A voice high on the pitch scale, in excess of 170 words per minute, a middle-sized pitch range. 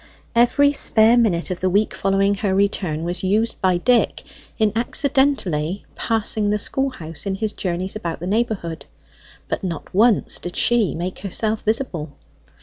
No: high, 200 Hz; average, 150 wpm; average, 4.2 semitones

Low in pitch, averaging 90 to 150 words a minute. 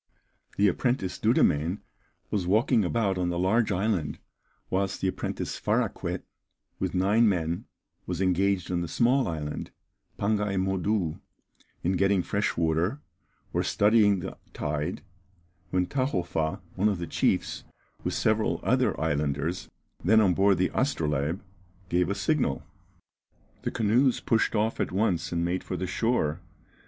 Yes: very low, 95 Hz; average, 140 wpm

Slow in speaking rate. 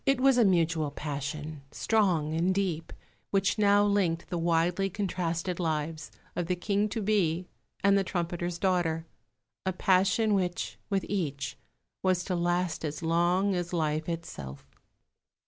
No: average, 145 wpm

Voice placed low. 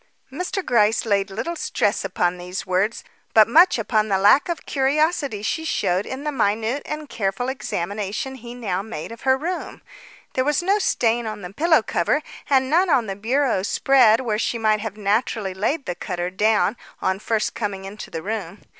No: high, 220 Hz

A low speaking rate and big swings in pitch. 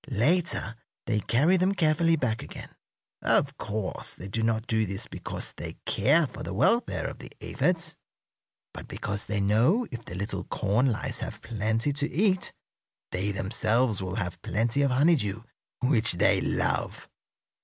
No: average, 155 wpm; wide, 6.1 semitones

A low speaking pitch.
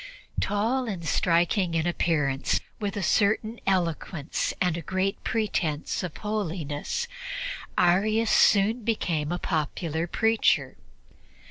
No: medium, 185 Hz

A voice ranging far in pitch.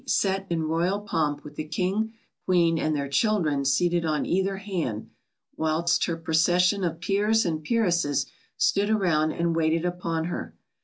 No: average, 3.4 semitones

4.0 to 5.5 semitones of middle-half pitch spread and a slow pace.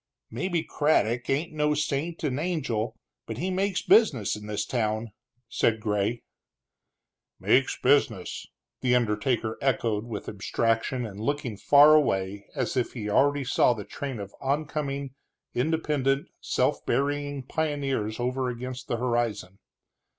Yes: average, 4.6 semitones; slow, 130 wpm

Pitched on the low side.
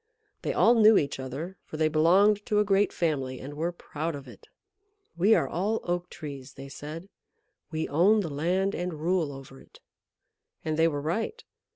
No: medium, 165 Hz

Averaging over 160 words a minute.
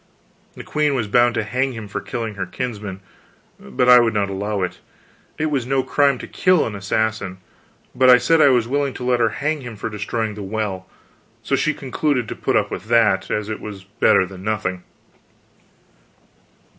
Yes: average, 195 wpm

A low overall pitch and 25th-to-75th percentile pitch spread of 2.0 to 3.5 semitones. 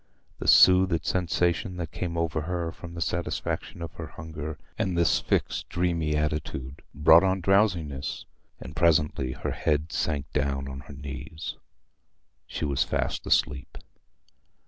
Yes: very low, 80 Hz; average, 2.8 semitones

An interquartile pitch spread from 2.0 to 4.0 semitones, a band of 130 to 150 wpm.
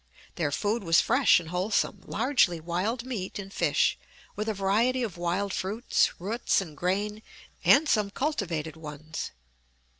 No: average, 4.7 semitones; average, 145 wpm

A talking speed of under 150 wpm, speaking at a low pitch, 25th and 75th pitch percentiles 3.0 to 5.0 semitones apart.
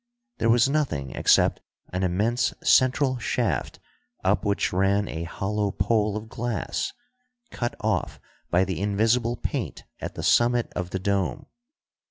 Yes: average, 140 wpm; low, 105 Hz; average, 4.0 semitones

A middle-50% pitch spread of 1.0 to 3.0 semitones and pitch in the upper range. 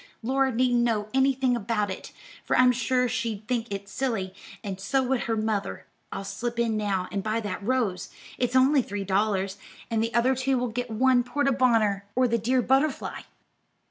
No: average, 3.6 semitones; high, 235 Hz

